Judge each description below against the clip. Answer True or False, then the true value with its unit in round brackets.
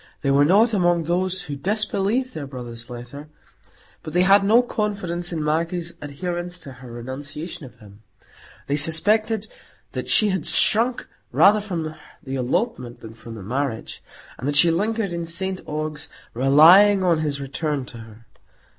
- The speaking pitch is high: False (160 Hz)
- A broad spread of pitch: True (5.7 semitones)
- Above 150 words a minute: True (160 wpm)